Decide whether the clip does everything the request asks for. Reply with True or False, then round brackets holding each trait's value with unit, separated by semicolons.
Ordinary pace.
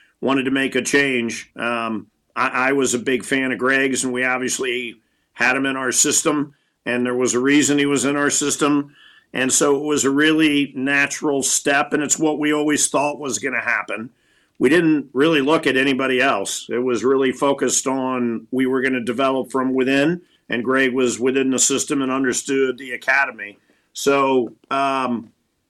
True (190 wpm)